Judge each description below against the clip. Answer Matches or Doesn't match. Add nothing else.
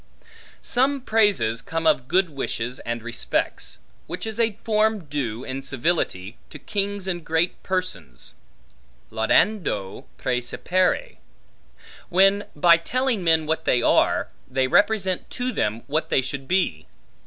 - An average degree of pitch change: Doesn't match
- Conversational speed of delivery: Doesn't match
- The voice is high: Doesn't match